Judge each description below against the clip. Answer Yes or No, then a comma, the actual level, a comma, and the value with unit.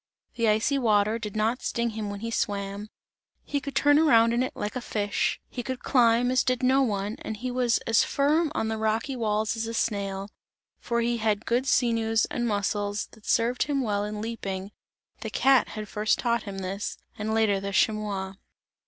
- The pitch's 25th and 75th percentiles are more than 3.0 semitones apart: No, average, 2.7 semitones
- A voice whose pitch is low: No, high, 225 Hz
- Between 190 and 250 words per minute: Yes, average, 195 wpm